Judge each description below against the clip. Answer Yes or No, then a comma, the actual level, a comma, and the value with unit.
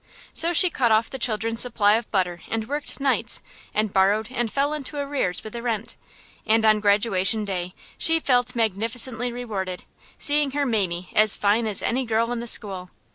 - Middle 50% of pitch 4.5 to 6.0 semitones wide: No, average, 3.4 semitones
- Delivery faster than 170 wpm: Yes, average, 185 wpm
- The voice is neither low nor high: No, high, 225 Hz